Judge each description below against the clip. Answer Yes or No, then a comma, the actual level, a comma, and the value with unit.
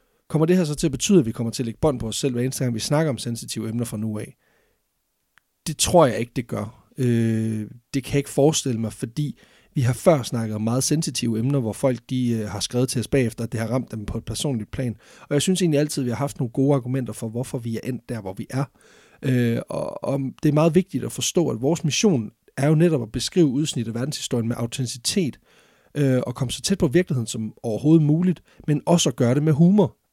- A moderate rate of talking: No, fast, 245 wpm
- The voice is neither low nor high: No, low, 130 Hz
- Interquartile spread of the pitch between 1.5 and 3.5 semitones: No, average, 4.2 semitones